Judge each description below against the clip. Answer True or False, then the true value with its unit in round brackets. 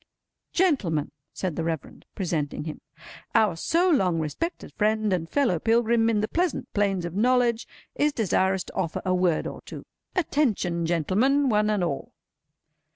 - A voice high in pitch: True (205 Hz)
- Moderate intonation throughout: False (5.9 semitones)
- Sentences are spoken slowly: False (155 wpm)